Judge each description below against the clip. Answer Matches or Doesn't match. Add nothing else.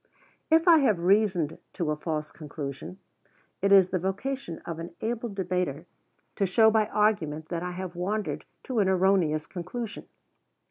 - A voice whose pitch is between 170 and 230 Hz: Matches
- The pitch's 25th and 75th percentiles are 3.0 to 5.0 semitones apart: Matches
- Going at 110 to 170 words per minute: Matches